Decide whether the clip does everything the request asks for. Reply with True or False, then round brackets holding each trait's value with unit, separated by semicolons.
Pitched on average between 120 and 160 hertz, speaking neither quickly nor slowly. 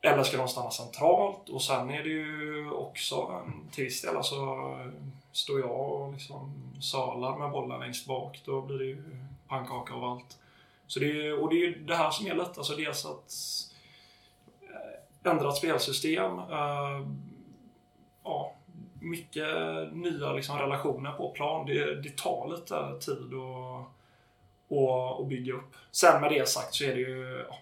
True (135 Hz; 155 wpm)